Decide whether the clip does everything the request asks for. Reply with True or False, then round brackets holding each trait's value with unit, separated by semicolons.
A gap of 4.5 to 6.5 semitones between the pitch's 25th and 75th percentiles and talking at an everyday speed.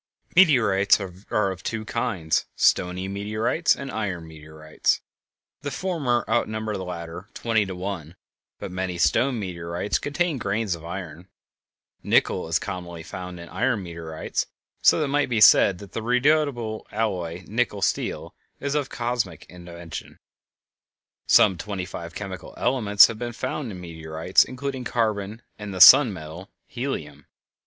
True (5.4 semitones; 145 wpm)